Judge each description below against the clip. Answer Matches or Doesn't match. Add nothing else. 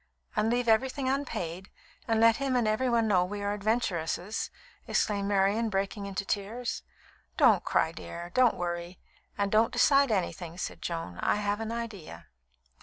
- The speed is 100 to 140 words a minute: Doesn't match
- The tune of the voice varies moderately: Matches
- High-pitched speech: Matches